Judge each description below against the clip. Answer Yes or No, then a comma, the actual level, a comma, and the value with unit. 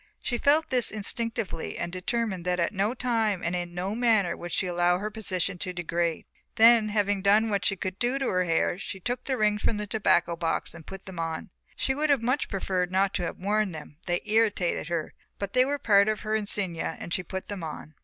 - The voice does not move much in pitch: No, average, 3.8 semitones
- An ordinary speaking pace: No, fast, 225 wpm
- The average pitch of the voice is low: No, high, 200 Hz